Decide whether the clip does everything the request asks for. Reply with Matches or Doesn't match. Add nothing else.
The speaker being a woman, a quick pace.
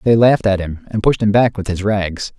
Doesn't match